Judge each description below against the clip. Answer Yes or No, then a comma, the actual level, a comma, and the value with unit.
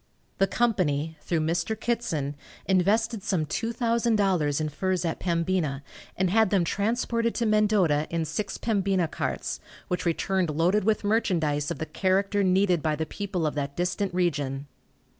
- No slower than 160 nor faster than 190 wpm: No, average, 150 wpm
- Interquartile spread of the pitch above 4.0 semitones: Yes, average, 4.6 semitones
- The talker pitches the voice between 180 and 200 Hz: Yes, medium, 185 Hz